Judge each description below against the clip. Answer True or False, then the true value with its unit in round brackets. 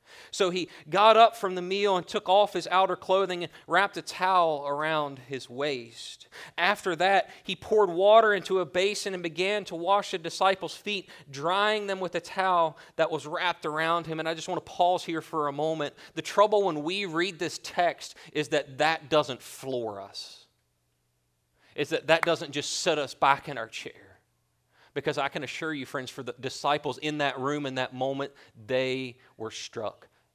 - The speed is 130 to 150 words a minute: False (190 wpm)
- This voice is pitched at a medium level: True (165 Hz)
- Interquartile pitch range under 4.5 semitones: False (4.9 semitones)